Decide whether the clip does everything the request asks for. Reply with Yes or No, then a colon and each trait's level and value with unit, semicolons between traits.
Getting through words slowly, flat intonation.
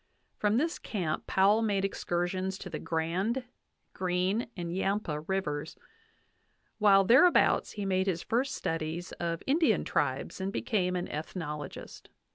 No: slow, 130 wpm; average, 3.7 semitones